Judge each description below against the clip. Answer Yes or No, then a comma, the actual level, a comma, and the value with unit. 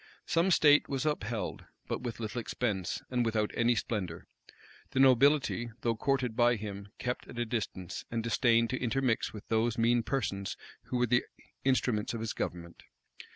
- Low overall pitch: Yes, low, 115 Hz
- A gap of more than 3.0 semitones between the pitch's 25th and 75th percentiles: No, narrow, 2.6 semitones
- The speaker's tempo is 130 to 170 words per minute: Yes, average, 165 wpm